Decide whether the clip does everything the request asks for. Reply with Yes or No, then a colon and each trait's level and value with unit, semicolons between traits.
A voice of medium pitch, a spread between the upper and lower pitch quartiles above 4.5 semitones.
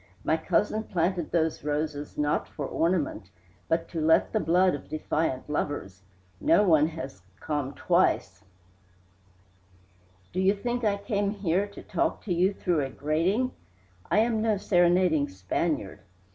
Yes: medium, 165 Hz; average, 5.1 semitones